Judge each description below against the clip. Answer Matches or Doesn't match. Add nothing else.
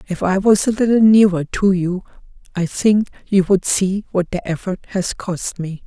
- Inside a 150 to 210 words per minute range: Matches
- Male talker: Doesn't match